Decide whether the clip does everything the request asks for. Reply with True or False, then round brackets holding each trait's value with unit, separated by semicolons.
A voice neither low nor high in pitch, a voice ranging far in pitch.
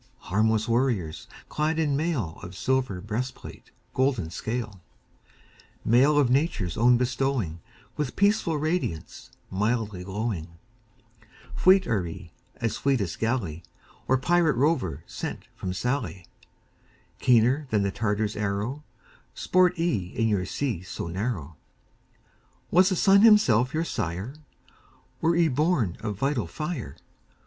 False (120 Hz; 7.1 semitones)